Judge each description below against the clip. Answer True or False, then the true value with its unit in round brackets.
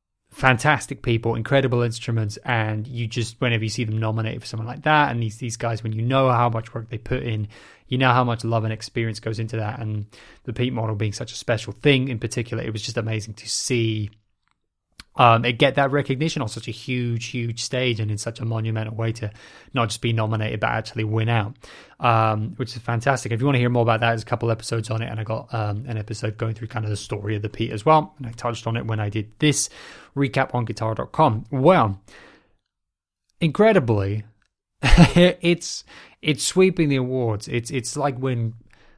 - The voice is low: True (115 Hz)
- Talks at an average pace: False (215 wpm)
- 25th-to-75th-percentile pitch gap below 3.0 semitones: True (2.5 semitones)